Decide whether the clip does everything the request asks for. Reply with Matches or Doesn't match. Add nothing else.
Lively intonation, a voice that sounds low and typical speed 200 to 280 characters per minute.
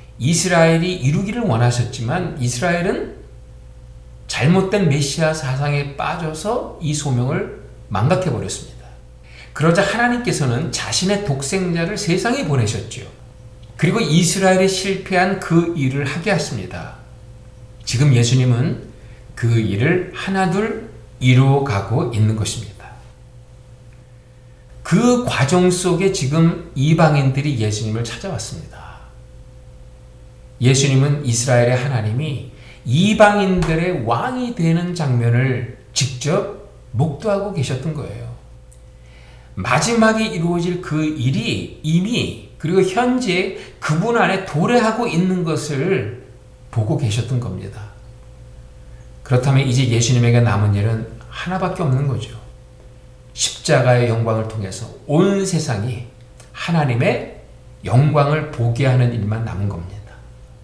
Matches